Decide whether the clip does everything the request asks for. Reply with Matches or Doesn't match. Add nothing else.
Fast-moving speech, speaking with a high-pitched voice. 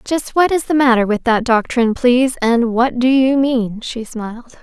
Matches